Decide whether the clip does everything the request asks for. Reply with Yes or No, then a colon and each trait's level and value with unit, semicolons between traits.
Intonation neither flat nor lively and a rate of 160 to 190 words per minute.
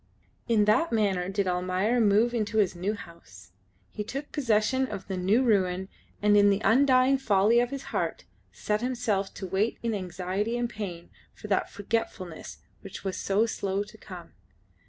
Yes: average, 3.4 semitones; average, 170 wpm